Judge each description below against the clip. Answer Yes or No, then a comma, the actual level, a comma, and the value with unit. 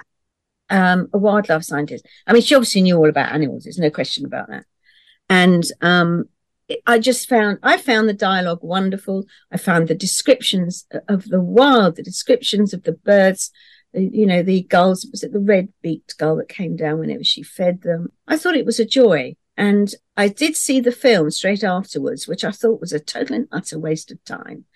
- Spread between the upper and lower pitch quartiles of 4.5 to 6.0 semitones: Yes, average, 5.1 semitones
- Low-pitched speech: No, high, 190 Hz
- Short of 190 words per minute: No, average, 200 wpm